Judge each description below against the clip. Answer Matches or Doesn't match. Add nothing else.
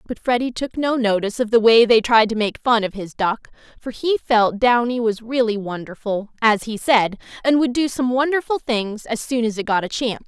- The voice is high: Matches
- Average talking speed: Doesn't match